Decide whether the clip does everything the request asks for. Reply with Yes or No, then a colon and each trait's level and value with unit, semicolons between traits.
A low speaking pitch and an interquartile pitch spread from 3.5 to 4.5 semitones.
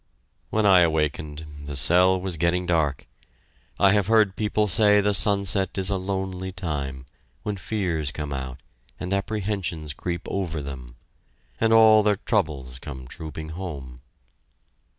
No: very low, 90 Hz; average, 4.9 semitones